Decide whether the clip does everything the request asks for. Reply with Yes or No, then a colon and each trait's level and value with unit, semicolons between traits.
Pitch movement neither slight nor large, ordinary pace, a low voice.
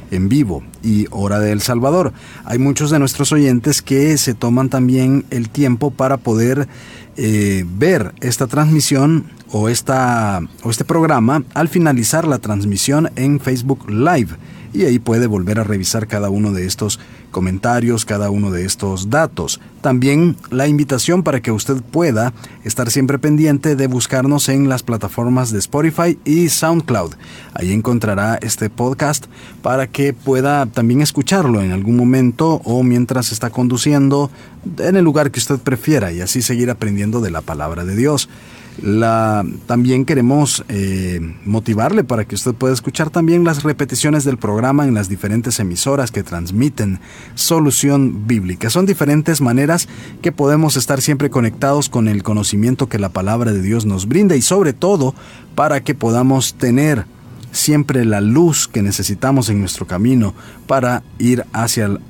Yes: average, 4.6 semitones; average, 155 wpm; low, 125 Hz